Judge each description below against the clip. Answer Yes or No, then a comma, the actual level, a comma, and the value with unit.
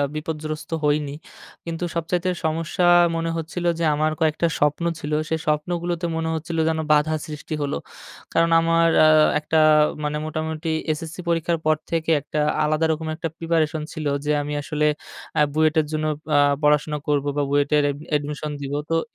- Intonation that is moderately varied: No, narrow, 1.6 semitones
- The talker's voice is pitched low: No, medium, 155 Hz